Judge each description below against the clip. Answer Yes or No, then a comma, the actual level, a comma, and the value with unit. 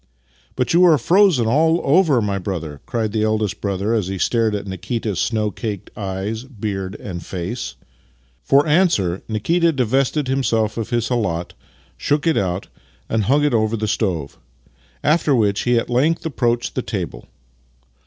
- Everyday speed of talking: Yes, average, 165 wpm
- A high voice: No, low, 110 Hz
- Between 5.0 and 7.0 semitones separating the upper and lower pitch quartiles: Yes, wide, 5.4 semitones